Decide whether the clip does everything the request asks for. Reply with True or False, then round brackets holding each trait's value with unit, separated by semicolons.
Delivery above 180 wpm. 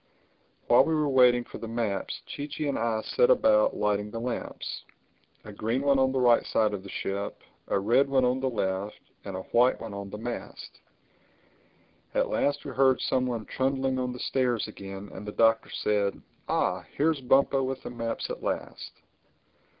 True (190 wpm)